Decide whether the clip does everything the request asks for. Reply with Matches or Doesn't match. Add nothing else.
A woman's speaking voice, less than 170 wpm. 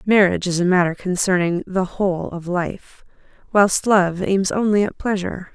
Matches